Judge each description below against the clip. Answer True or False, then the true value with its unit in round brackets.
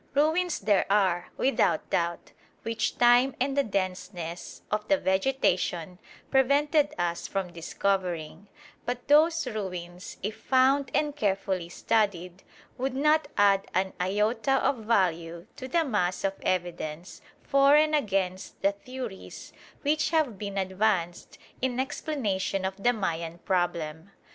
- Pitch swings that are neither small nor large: False (6.7 semitones)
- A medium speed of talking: False (130 wpm)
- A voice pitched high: True (200 Hz)